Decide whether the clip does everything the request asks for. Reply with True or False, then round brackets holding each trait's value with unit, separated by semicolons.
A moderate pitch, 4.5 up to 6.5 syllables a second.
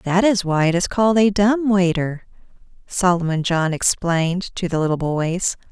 True (180 Hz; 4.7 syllables/s)